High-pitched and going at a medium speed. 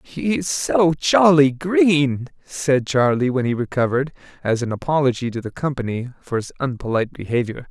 No: low, 135 Hz; average, 155 wpm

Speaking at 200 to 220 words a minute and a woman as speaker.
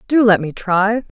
Yes: fast, 205 wpm; female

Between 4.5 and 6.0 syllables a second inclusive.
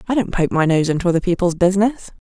No: 7.1 syllables/s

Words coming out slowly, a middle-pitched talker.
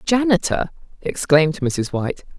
Yes: slow, 100 wpm; medium, 170 Hz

